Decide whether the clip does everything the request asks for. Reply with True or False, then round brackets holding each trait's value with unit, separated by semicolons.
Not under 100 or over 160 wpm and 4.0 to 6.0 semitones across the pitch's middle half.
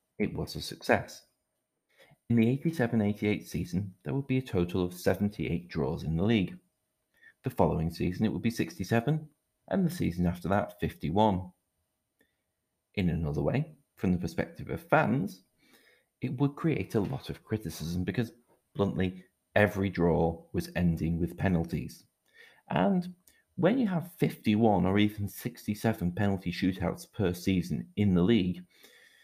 True (145 wpm; 5.0 semitones)